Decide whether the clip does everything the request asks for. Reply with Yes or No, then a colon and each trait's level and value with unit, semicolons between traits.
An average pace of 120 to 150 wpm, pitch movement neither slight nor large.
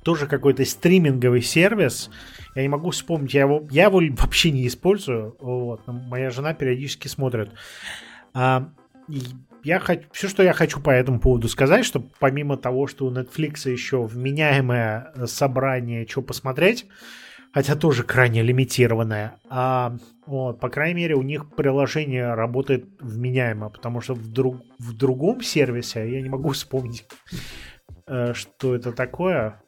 Yes: average, 145 wpm; average, 3.1 semitones